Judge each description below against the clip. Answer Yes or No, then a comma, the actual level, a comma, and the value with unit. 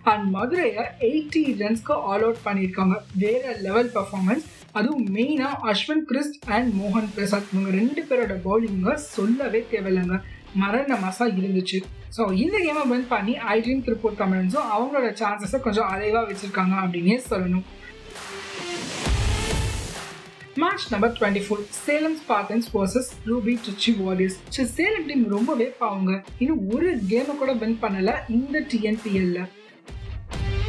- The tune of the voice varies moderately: Yes, average, 4.3 semitones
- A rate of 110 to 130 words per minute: Yes, average, 125 wpm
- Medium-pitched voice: No, high, 220 Hz